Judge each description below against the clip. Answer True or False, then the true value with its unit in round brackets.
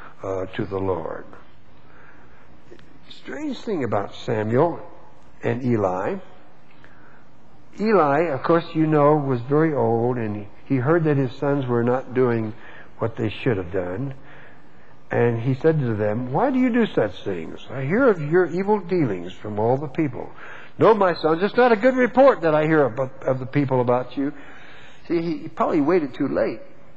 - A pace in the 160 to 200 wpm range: True (170 wpm)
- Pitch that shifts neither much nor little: False (6.5 semitones)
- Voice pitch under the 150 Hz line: True (135 Hz)